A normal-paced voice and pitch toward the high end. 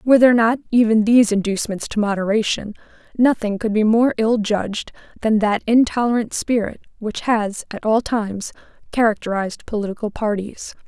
Yes: average, 145 wpm; high, 220 Hz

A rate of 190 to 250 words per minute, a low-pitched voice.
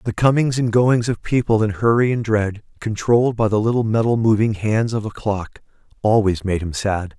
Yes: average, 200 wpm; low, 110 Hz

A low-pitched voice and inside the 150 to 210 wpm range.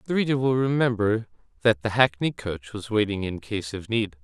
Yes: low, 110 Hz; average, 200 wpm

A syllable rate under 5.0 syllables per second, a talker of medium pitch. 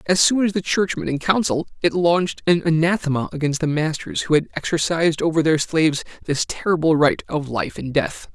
No: 5.5 syllables/s; medium, 160 Hz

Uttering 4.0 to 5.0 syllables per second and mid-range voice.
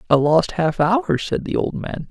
Yes: 4.2 syllables/s; medium, 175 Hz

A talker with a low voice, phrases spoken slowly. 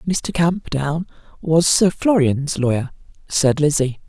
No: medium, 155 Hz; slow, 120 wpm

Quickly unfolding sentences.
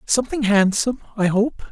No: average, 140 wpm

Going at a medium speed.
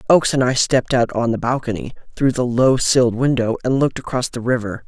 No: fast, 220 wpm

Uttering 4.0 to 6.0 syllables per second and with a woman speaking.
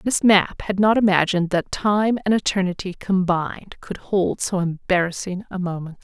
Yes: 4.8 syllables/s; female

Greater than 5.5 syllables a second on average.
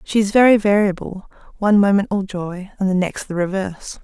Yes: 5.7 syllables/s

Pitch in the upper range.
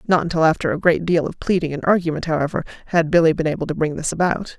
No: medium, 165 Hz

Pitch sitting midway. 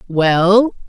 No: high, 195 Hz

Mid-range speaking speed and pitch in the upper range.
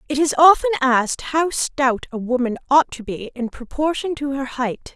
Yes: average, 195 wpm; very high, 270 Hz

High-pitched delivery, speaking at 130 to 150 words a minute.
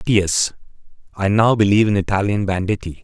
No: low, 100 Hz; average, 140 wpm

